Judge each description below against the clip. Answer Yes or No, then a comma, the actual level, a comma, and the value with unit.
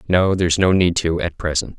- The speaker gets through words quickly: Yes, fast, 235 wpm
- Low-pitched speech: Yes, very low, 90 Hz